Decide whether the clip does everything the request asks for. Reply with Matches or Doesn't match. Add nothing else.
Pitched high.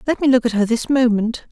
Matches